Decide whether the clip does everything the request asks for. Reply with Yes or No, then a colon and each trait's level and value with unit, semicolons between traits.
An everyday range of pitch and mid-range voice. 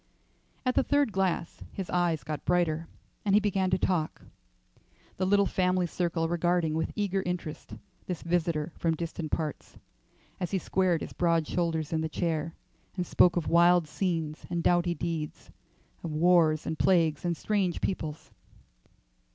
No: narrow, 2.2 semitones; medium, 170 Hz